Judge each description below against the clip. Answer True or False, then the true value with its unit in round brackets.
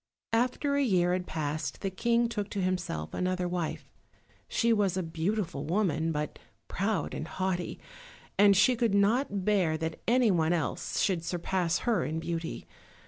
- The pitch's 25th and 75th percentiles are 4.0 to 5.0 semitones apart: True (4.3 semitones)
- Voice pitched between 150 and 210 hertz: True (185 Hz)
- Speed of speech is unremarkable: True (155 wpm)